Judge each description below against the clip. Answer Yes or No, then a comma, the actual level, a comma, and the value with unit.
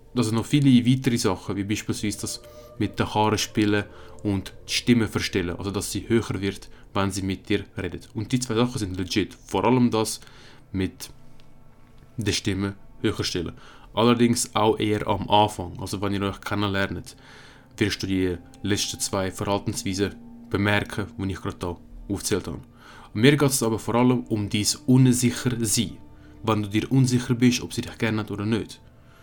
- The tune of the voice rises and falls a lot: No, average, 3.4 semitones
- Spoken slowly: No, average, 180 wpm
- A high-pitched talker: No, low, 110 Hz